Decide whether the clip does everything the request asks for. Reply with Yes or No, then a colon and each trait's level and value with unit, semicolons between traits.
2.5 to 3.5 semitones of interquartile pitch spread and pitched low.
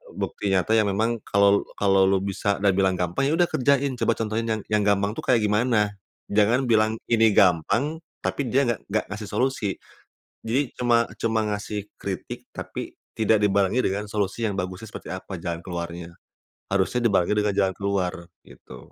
Yes: average, 2.9 semitones; low, 105 Hz